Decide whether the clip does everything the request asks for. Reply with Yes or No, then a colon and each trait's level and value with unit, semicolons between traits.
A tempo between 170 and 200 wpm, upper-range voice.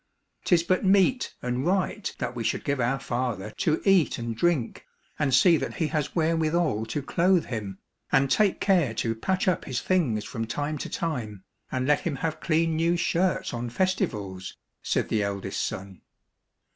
No: average, 180 wpm; medium, 145 Hz